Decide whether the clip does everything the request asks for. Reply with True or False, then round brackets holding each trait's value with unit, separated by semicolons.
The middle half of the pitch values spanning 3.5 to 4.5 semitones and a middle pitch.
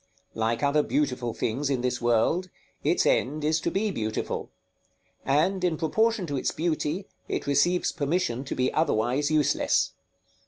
False (5.2 semitones; 145 Hz)